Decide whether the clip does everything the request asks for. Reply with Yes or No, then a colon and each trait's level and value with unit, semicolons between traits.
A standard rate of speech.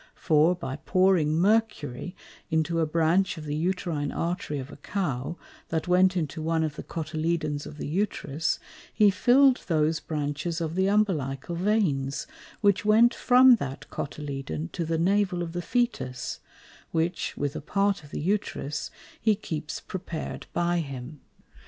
Yes: average, 150 wpm